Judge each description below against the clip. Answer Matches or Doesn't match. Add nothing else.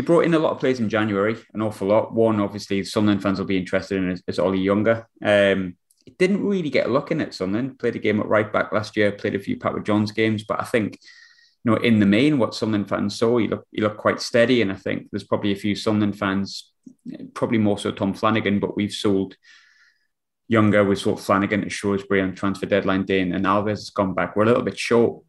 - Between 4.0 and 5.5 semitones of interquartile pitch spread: Doesn't match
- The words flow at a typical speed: Doesn't match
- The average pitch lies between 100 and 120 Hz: Matches